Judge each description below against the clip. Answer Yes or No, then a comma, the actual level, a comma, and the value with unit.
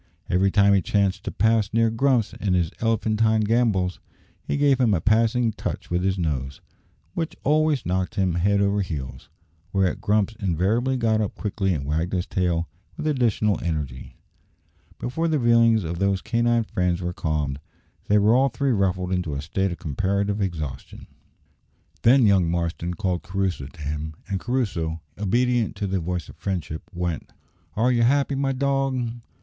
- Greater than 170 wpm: No, average, 165 wpm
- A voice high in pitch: No, low, 100 Hz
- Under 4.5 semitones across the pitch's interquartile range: No, average, 4.8 semitones